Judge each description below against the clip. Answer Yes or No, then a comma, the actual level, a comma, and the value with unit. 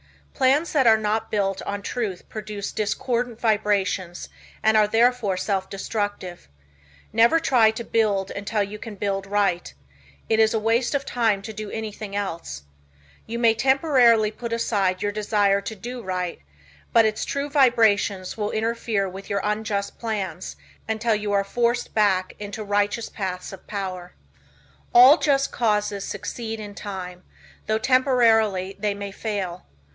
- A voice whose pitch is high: Yes, high, 210 Hz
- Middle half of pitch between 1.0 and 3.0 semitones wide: Yes, narrow, 2.5 semitones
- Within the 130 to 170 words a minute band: Yes, average, 150 wpm